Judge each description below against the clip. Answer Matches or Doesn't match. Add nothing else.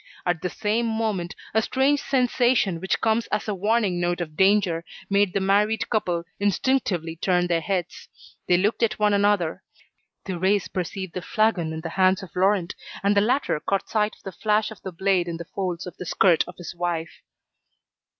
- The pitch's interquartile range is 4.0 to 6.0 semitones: Doesn't match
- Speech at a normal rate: Matches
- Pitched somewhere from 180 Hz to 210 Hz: Matches